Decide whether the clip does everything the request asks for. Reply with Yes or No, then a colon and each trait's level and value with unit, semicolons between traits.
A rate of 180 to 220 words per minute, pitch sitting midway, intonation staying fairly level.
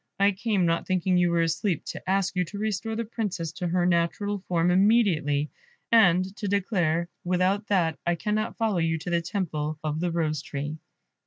No: average, 185 wpm; medium, 180 Hz; average, 3.4 semitones